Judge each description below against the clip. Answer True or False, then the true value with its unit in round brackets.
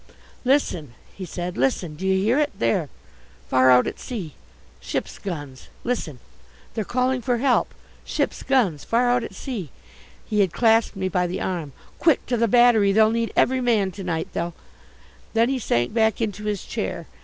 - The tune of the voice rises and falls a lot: True (5.7 semitones)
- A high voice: True (210 Hz)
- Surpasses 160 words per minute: True (180 wpm)